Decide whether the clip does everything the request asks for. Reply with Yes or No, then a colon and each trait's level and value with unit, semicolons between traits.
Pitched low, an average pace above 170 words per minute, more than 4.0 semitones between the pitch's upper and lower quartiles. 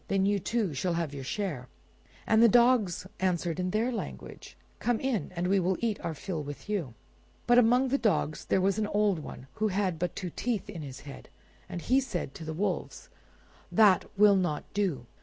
No: high, 190 Hz; average, 200 wpm; average, 4.5 semitones